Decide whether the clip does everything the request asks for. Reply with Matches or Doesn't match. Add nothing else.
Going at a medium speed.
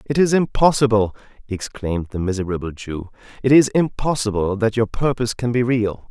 Matches